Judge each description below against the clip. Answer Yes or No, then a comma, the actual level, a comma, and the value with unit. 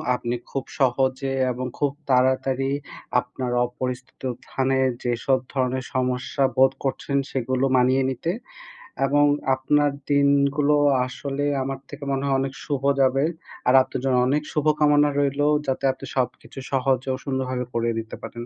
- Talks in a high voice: No, low, 135 Hz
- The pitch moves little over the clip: Yes, narrow, 1.6 semitones